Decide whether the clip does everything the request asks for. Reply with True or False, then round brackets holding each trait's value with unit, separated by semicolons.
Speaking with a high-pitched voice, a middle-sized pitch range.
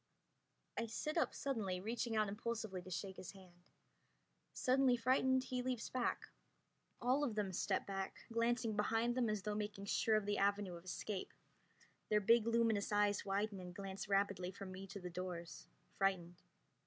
True (205 Hz; 3.3 semitones)